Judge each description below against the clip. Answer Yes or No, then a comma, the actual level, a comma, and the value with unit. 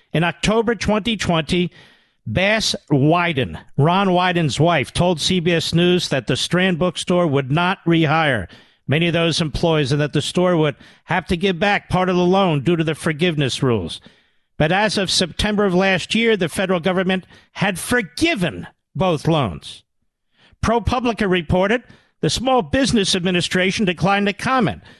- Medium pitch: Yes, medium, 180 Hz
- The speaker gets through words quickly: No, average, 150 wpm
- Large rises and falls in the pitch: No, average, 3.5 semitones